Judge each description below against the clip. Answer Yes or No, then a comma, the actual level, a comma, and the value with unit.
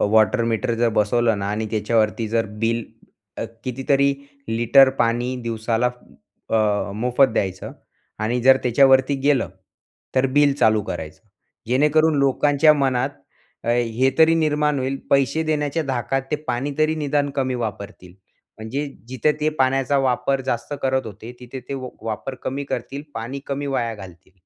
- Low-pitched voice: Yes, low, 130 Hz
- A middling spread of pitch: Yes, average, 3.6 semitones